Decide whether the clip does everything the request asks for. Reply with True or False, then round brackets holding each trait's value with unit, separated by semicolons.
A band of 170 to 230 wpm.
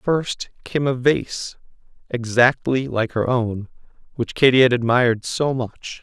False (140 wpm)